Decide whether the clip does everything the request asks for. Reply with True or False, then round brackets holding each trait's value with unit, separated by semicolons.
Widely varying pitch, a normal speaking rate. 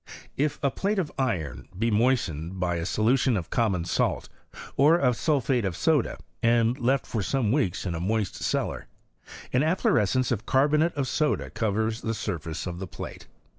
True (6.0 semitones; 170 wpm)